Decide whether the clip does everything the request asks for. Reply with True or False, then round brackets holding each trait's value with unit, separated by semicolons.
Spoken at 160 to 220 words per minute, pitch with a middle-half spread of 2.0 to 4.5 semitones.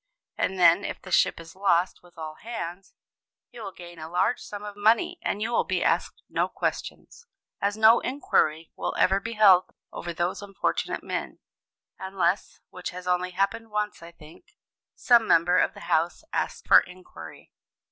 True (175 wpm; 3.4 semitones)